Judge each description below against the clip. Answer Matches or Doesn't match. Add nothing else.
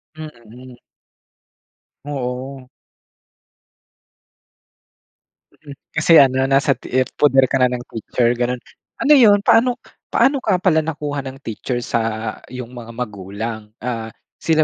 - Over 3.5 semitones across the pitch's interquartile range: Matches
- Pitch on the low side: Matches